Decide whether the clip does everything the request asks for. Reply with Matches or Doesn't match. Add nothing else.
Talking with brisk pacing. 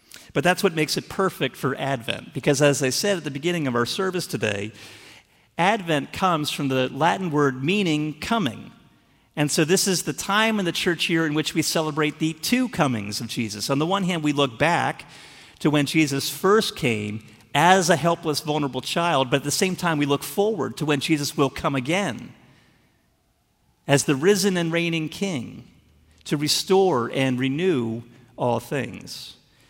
Doesn't match